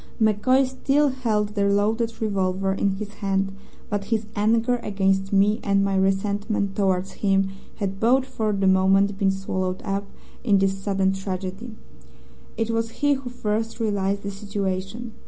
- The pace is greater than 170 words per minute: No, average, 155 wpm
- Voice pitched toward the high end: Yes, high, 200 Hz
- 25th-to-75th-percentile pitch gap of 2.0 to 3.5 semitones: Yes, narrow, 2.5 semitones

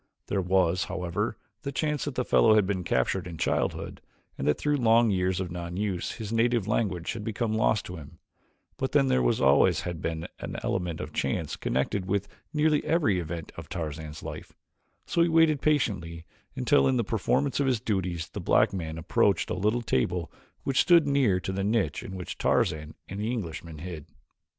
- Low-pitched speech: Yes, very low, 95 Hz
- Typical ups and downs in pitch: No, wide, 5.8 semitones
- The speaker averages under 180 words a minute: No, average, 190 wpm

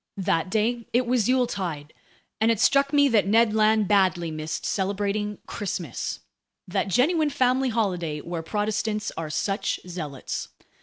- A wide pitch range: No, average, 4.7 semitones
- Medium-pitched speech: No, high, 210 Hz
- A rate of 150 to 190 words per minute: No, average, 140 wpm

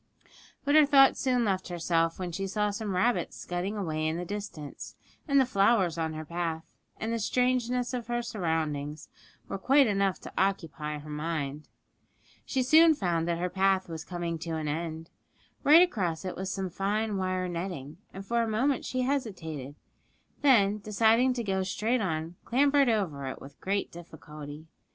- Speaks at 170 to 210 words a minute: Yes, average, 175 wpm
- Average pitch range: No, wide, 6.1 semitones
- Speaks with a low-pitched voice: No, high, 190 Hz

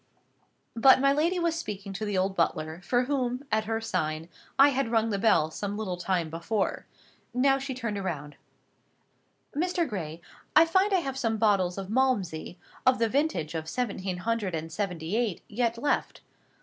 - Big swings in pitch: Yes, wide, 6.4 semitones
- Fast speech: No, average, 175 wpm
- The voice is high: Yes, high, 220 Hz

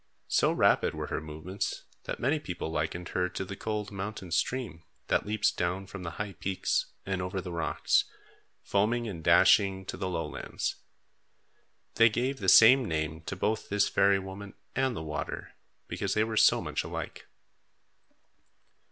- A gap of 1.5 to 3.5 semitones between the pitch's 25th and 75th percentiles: Yes, average, 3.2 semitones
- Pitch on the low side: Yes, very low, 95 Hz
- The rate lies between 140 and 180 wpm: Yes, average, 160 wpm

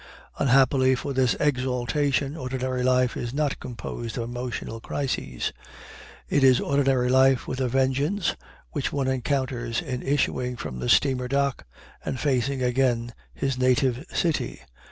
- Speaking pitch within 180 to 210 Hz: No, low, 130 Hz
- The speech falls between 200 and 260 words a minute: No, slow, 135 wpm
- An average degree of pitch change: No, narrow, 1.8 semitones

